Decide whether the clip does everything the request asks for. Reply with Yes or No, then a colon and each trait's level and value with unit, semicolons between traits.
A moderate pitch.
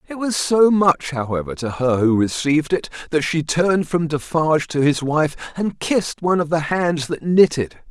Yes: medium, 160 Hz